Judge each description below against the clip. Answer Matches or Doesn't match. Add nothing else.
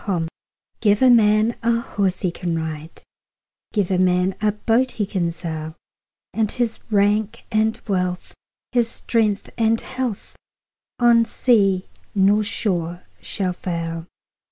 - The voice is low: Doesn't match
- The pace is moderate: Doesn't match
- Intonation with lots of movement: Doesn't match